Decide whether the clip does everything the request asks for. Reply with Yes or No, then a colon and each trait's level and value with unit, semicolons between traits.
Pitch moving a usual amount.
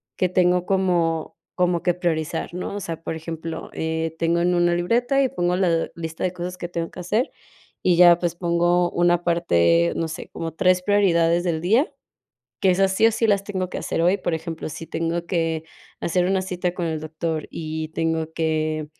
No: narrow, 1.8 semitones